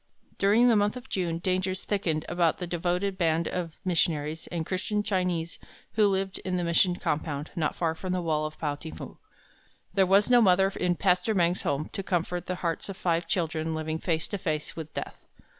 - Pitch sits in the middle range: Yes, medium, 175 Hz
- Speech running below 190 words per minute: No, average, 200 wpm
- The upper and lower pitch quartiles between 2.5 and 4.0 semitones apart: Yes, average, 2.9 semitones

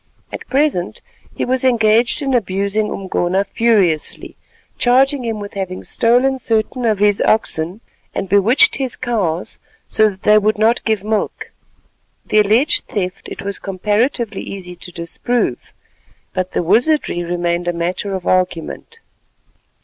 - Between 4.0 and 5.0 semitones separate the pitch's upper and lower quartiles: Yes, average, 4.3 semitones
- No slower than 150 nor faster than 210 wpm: No, average, 140 wpm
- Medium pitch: No, high, 210 Hz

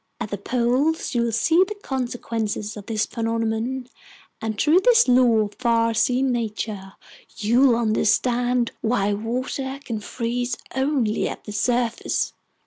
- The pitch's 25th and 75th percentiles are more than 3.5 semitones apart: No, narrow, 2.6 semitones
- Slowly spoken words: Yes, slow, 130 wpm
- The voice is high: Yes, high, 235 Hz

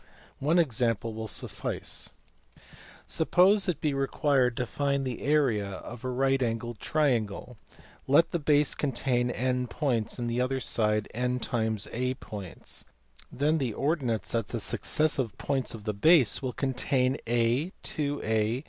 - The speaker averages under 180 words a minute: Yes, average, 140 wpm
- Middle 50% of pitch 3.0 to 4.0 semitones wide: Yes, average, 3.6 semitones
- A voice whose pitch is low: Yes, low, 125 Hz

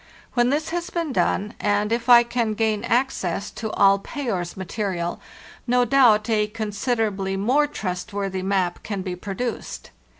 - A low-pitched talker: No, high, 215 Hz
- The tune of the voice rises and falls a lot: No, average, 3.8 semitones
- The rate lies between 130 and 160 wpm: Yes, average, 155 wpm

